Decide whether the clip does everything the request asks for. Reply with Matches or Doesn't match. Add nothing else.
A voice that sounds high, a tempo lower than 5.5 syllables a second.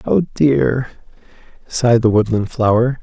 Doesn't match